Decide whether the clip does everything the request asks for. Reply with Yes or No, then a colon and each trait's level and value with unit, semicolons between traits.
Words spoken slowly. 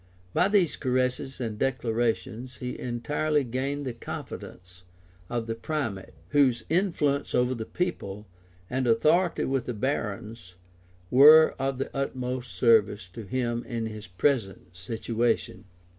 Yes: slow, 130 wpm